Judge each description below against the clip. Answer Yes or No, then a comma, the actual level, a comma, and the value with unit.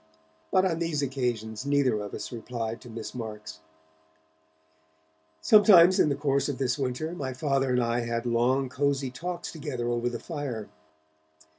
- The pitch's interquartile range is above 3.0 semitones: Yes, average, 3.5 semitones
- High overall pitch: No, low, 130 Hz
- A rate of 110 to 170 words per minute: Yes, average, 155 wpm